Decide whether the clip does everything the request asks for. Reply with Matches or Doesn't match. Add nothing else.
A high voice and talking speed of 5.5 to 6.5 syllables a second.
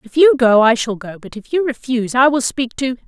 Matches